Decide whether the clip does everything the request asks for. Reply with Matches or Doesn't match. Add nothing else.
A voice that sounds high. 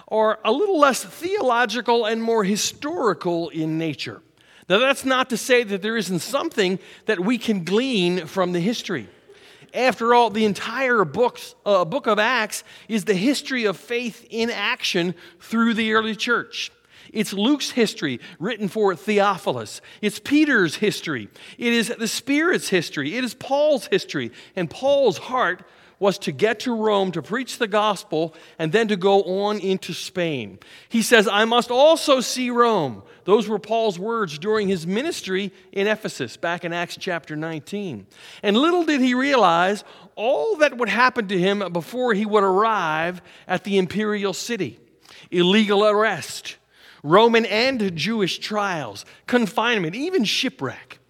Matches